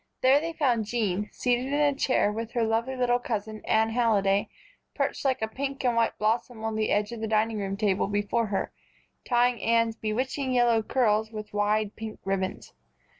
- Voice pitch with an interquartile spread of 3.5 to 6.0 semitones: No, narrow, 2.6 semitones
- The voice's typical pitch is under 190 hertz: No, high, 225 Hz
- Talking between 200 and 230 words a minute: No, average, 180 wpm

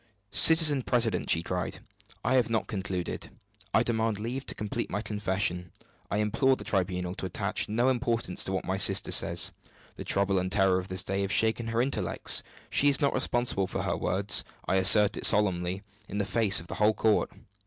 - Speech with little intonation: No, average, 3.6 semitones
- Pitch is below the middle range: Yes, low, 105 Hz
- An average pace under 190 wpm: No, average, 195 wpm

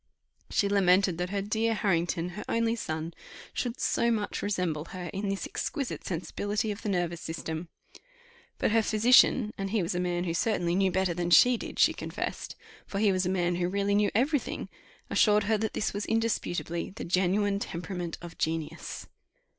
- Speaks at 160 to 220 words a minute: Yes, average, 185 wpm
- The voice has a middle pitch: No, high, 195 Hz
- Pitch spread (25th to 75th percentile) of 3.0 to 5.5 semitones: Yes, average, 3.3 semitones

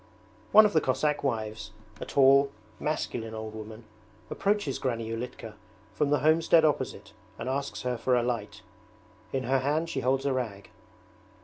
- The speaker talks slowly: No, average, 155 wpm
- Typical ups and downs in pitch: Yes, average, 4.4 semitones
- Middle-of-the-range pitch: No, low, 130 Hz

